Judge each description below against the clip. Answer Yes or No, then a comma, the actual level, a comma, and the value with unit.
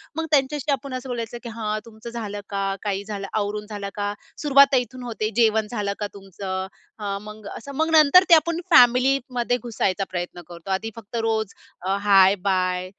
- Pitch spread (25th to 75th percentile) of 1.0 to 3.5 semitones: No, average, 3.9 semitones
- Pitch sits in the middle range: No, high, 215 Hz